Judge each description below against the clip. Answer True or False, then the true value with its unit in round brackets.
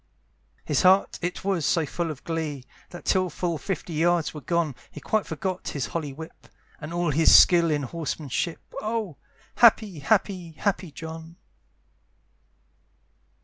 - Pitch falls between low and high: True (170 Hz)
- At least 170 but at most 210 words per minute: False (145 wpm)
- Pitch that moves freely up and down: False (3.0 semitones)